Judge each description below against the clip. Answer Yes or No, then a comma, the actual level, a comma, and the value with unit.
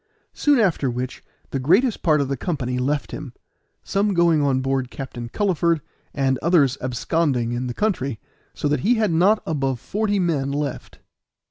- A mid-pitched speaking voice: Yes, medium, 145 Hz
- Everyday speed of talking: Yes, average, 165 wpm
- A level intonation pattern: No, average, 5.2 semitones